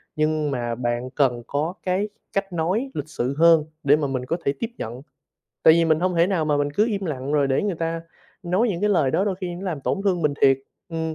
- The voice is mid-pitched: Yes, medium, 160 Hz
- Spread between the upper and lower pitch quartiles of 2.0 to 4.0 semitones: No, average, 4.6 semitones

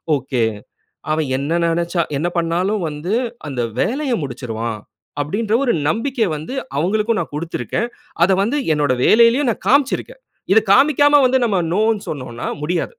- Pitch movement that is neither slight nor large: No, wide, 7.7 semitones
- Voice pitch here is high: No, medium, 180 Hz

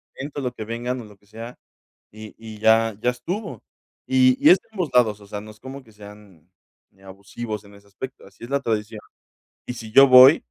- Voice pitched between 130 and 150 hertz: No, low, 115 Hz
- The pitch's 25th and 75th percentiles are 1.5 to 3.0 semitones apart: No, average, 3.5 semitones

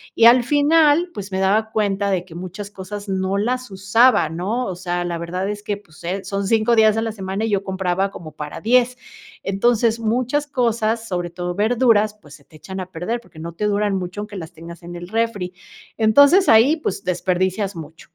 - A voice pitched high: Yes, high, 200 Hz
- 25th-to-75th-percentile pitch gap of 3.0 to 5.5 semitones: Yes, average, 3.9 semitones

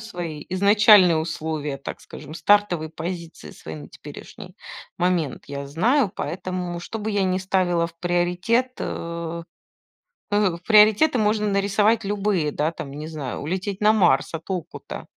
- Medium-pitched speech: Yes, medium, 180 Hz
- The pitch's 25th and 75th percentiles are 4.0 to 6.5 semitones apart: Yes, average, 4.3 semitones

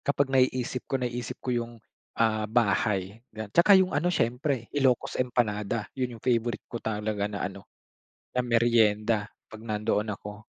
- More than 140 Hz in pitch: No, low, 115 Hz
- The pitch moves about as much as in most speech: Yes, average, 3.0 semitones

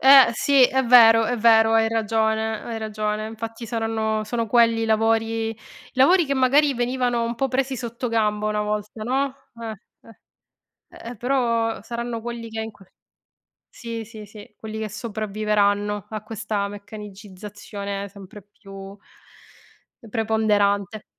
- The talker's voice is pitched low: No, high, 225 Hz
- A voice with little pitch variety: Yes, narrow, 1.9 semitones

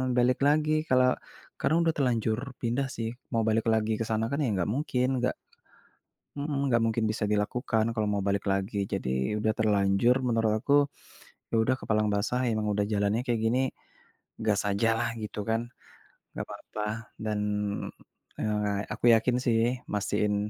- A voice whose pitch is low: Yes, low, 110 Hz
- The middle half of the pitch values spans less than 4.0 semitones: Yes, average, 2.8 semitones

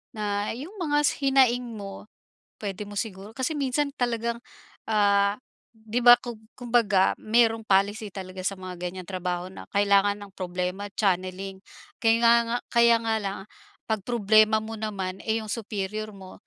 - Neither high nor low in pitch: No, high, 215 Hz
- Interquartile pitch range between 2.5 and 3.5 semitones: Yes, average, 3.1 semitones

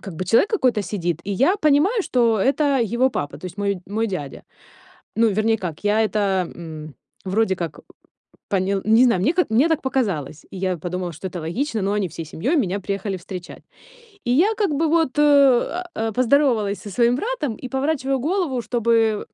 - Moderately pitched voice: No, high, 220 Hz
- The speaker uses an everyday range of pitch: No, wide, 6.2 semitones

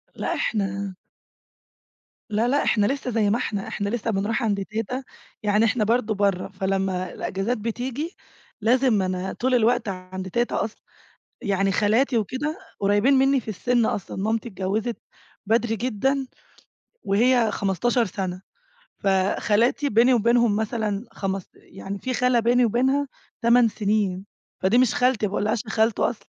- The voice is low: No, high, 220 Hz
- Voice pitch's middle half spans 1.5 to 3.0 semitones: No, average, 3.6 semitones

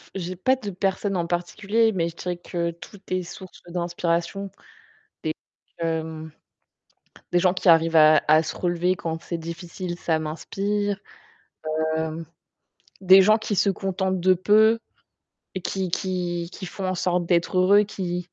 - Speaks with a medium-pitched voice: Yes, medium, 180 Hz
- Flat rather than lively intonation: Yes, narrow, 2.2 semitones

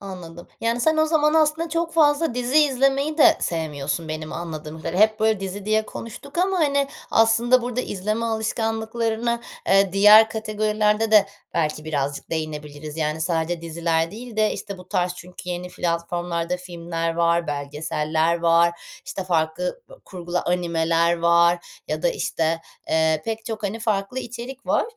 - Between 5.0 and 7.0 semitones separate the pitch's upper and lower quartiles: Yes, wide, 5.5 semitones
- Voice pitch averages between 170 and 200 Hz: Yes, medium, 185 Hz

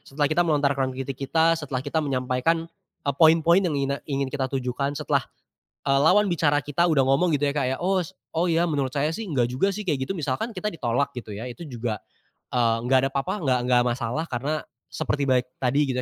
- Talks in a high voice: No, medium, 140 Hz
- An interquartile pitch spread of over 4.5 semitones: No, average, 3.9 semitones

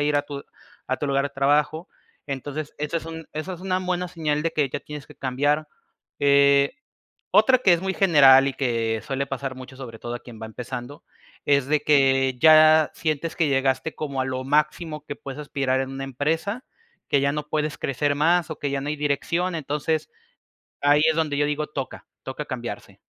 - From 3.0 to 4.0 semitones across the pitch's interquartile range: No, narrow, 2.4 semitones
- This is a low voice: No, medium, 145 Hz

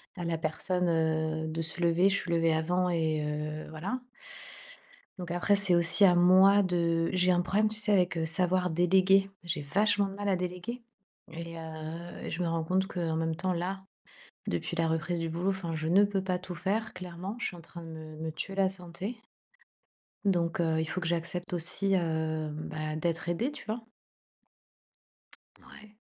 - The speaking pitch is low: No, medium, 175 Hz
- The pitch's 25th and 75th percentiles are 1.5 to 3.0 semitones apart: Yes, average, 2.7 semitones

